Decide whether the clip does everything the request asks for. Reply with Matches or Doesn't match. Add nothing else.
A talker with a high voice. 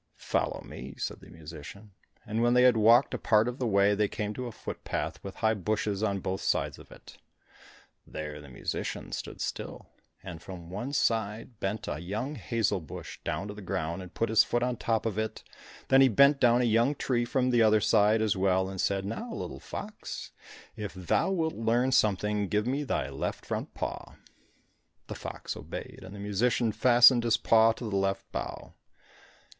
Doesn't match